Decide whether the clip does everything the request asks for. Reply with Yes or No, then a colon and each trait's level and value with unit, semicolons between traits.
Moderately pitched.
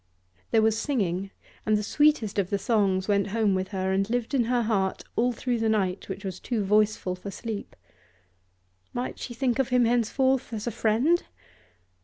No: high, 220 Hz